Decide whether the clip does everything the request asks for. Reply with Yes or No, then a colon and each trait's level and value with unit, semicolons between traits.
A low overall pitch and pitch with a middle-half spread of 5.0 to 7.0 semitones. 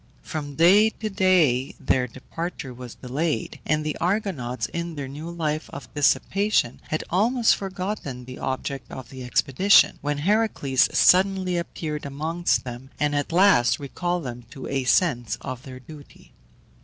No: medium, 150 Hz; wide, 5.6 semitones